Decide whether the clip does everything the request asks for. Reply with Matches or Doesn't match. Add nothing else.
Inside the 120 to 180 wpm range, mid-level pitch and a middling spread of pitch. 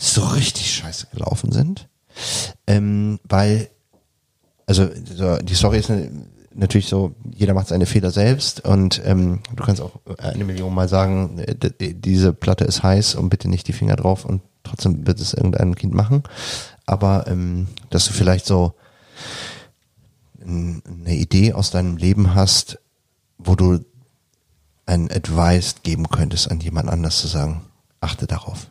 Doesn't match